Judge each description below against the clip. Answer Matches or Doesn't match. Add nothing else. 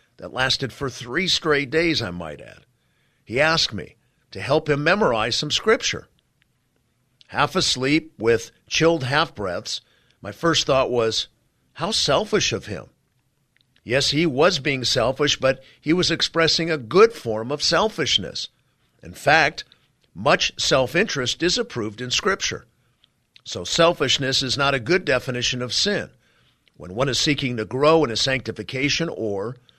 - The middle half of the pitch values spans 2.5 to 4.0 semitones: Doesn't match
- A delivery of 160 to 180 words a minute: Doesn't match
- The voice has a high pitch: Doesn't match